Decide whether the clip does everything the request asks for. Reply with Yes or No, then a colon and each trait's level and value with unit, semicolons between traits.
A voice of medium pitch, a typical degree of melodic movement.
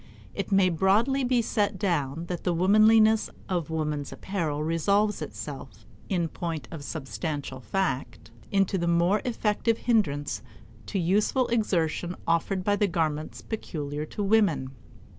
Yes: medium, 180 Hz; average, 4.9 semitones